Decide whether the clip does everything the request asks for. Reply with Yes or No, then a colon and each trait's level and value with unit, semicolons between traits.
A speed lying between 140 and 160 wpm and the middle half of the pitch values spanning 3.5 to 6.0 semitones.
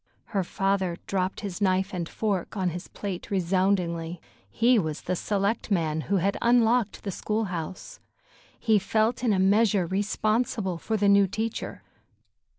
No: average, 150 wpm; average, 2.8 semitones